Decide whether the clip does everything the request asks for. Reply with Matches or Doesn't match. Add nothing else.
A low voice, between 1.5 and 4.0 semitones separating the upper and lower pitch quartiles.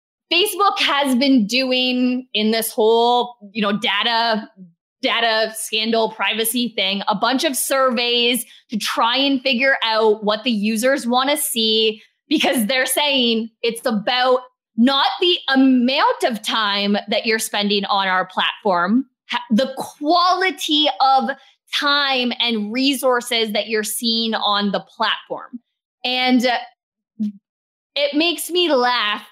Doesn't match